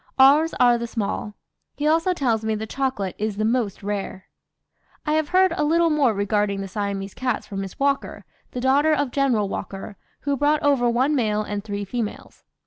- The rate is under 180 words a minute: No, average, 190 wpm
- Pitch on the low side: No, high, 240 Hz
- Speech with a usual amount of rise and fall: No, wide, 5.7 semitones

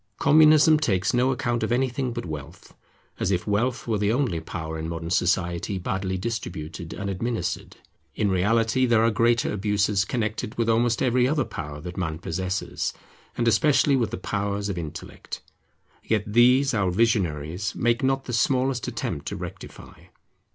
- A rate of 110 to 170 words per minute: Yes, average, 160 wpm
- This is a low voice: Yes, low, 105 Hz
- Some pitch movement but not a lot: Yes, average, 4.9 semitones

